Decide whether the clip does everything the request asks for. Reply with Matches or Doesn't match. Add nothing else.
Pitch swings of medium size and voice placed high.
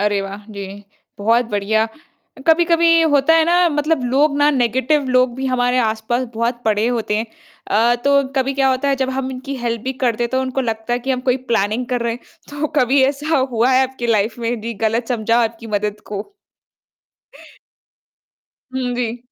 Matches